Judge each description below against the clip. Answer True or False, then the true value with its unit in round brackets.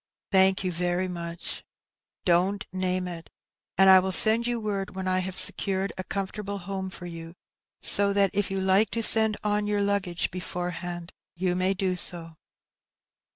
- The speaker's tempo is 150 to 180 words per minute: True (165 wpm)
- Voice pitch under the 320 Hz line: True (190 Hz)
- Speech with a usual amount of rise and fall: False (2.1 semitones)